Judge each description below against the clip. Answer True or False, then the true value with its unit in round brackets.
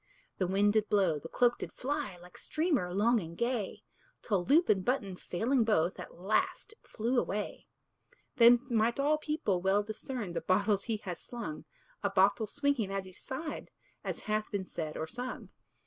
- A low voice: False (210 Hz)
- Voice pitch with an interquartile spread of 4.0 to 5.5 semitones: True (4.7 semitones)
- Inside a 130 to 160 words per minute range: False (180 wpm)